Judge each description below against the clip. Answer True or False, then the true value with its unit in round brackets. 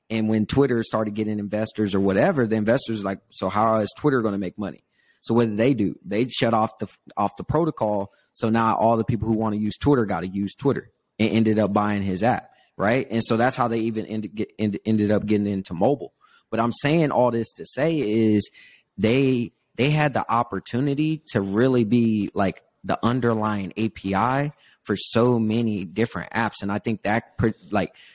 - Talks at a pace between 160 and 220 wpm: True (205 wpm)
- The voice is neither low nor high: False (110 Hz)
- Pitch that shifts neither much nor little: False (2.3 semitones)